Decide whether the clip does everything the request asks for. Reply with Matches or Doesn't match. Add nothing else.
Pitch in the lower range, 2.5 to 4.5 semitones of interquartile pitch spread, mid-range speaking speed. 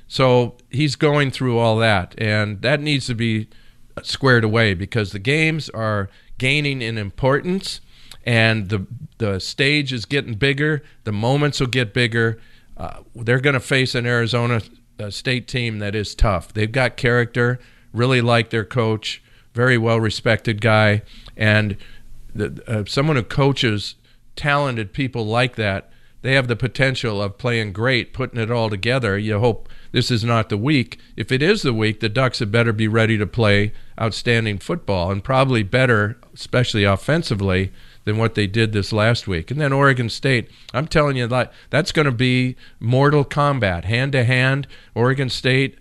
Matches